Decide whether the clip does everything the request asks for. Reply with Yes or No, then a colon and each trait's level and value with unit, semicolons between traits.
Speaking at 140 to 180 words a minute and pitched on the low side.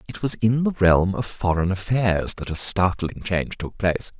No: average, 200 wpm; low, 100 Hz